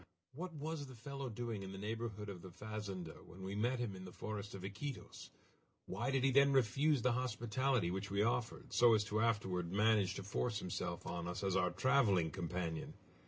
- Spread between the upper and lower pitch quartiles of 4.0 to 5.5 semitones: Yes, average, 4.8 semitones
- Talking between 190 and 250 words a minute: Yes, average, 200 wpm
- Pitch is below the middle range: Yes, low, 105 Hz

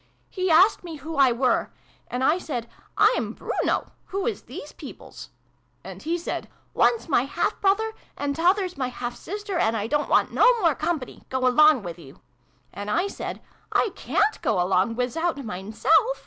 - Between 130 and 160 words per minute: No, average, 195 wpm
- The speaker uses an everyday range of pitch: No, wide, 7.1 semitones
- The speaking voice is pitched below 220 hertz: No, very high, 290 Hz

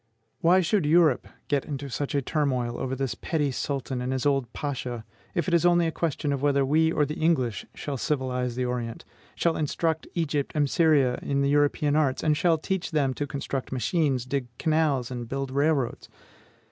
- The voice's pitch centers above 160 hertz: No, medium, 140 Hz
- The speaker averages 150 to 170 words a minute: No, average, 185 wpm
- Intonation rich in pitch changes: No, average, 3.3 semitones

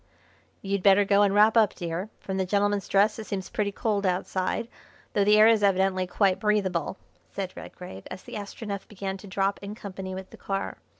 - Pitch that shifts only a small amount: Yes, narrow, 1.6 semitones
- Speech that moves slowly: No, average, 195 wpm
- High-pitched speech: Yes, high, 200 Hz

